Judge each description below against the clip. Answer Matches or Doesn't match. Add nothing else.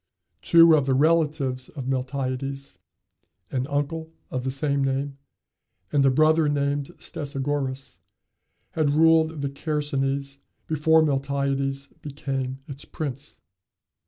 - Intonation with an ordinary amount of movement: Doesn't match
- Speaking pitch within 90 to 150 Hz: Matches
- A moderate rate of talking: Doesn't match